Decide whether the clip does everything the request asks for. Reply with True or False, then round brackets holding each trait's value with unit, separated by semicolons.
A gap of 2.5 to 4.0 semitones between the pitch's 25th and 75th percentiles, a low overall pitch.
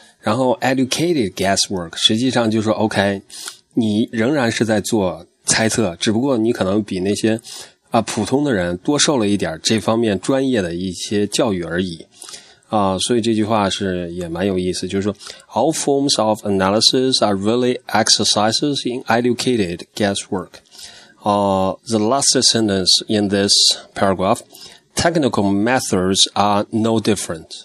True (2.8 semitones; 110 Hz)